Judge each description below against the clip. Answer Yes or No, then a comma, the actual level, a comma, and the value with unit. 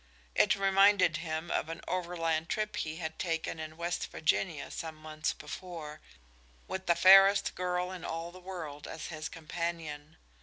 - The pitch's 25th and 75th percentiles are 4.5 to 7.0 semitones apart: No, narrow, 2.5 semitones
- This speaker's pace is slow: No, average, 155 wpm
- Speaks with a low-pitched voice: No, medium, 170 Hz